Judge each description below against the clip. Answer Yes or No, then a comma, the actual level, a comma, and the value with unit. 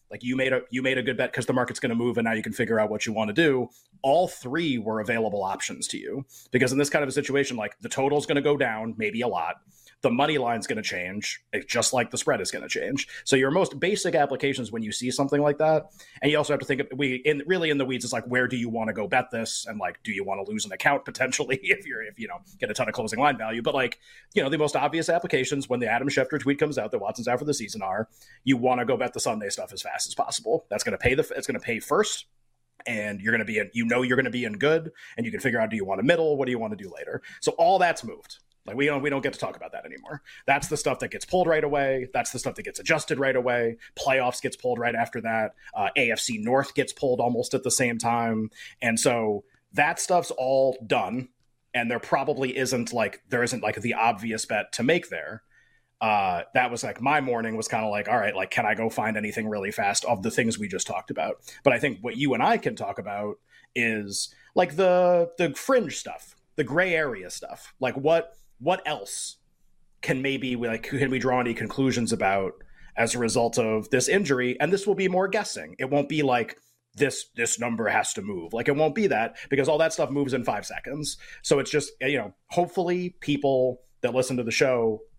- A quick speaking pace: Yes, fast, 260 wpm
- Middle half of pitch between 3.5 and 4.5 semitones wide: Yes, average, 4.0 semitones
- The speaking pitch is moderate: No, low, 130 Hz